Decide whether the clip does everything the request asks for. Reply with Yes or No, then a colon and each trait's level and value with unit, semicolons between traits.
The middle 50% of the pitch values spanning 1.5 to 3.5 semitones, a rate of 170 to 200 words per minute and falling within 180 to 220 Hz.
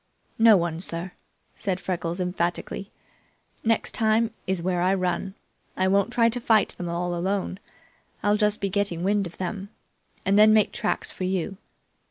No: average, 2.8 semitones; average, 160 wpm; high, 190 Hz